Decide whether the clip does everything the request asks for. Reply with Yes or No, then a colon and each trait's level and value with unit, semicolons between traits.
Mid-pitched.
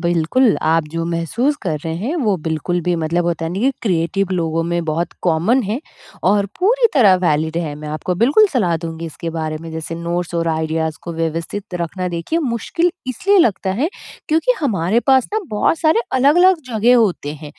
Yes: medium, 175 Hz